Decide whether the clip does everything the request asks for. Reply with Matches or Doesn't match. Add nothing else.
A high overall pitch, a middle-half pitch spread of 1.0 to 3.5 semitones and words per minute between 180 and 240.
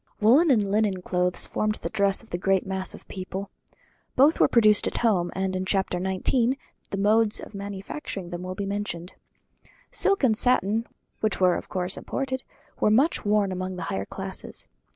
Matches